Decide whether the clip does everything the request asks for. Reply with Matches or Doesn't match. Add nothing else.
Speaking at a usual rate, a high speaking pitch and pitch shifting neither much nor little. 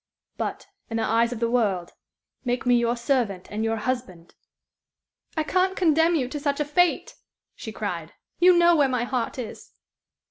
Matches